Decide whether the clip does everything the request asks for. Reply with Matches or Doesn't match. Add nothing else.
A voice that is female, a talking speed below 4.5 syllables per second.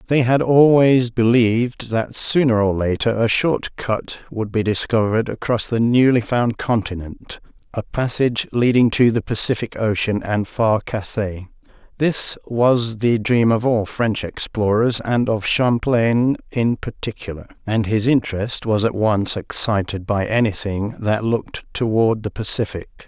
Doesn't match